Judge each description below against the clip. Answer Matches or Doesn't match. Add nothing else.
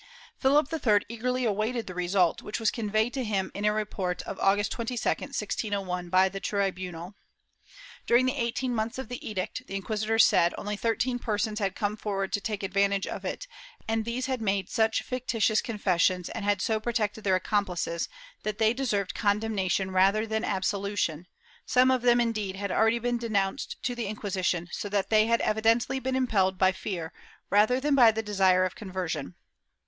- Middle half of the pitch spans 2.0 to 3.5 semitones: Matches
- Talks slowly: Doesn't match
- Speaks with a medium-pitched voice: Doesn't match